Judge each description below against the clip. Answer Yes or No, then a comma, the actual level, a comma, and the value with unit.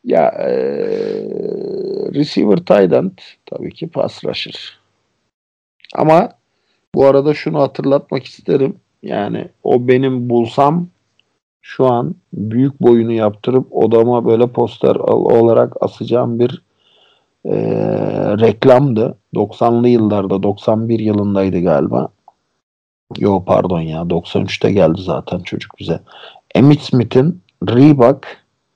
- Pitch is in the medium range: No, low, 125 Hz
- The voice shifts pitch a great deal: No, average, 4.3 semitones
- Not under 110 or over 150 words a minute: No, slow, 95 wpm